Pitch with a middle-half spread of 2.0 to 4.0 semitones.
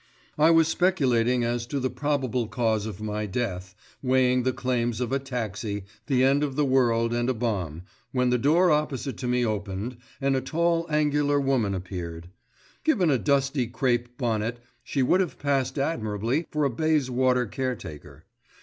Yes: average, 3.7 semitones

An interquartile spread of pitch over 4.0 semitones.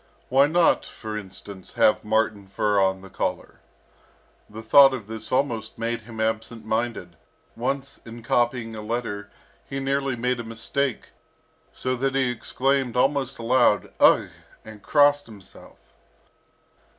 No: average, 3.5 semitones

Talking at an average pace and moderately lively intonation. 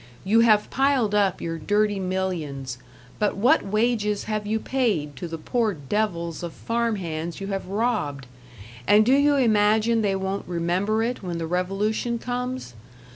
Yes: average, 160 wpm; average, 4.5 semitones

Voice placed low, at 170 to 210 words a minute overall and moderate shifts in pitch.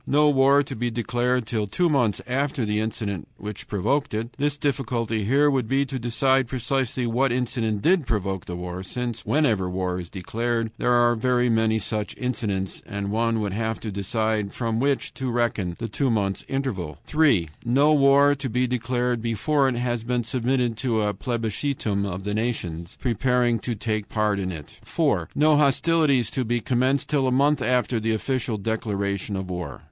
Yes: low, 120 Hz; average, 185 wpm; average, 3.9 semitones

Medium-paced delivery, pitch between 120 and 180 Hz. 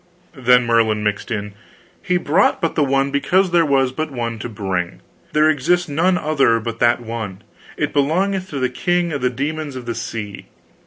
Yes: average, 195 wpm; low, 135 Hz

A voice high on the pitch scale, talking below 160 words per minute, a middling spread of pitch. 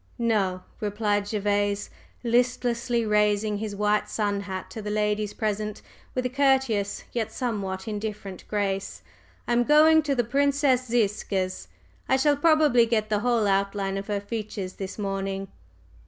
Yes: high, 210 Hz; average, 140 wpm; average, 3.2 semitones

